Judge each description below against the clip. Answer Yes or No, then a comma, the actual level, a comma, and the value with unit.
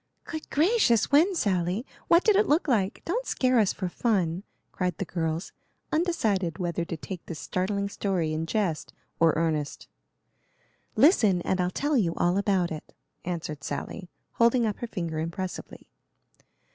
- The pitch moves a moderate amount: No, wide, 6.1 semitones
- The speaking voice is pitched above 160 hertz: Yes, high, 190 Hz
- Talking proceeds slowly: No, average, 155 wpm